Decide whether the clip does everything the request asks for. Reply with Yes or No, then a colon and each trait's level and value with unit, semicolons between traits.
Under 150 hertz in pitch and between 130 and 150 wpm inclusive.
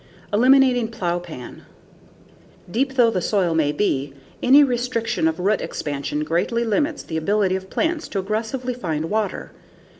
No: high, 210 Hz; average, 140 wpm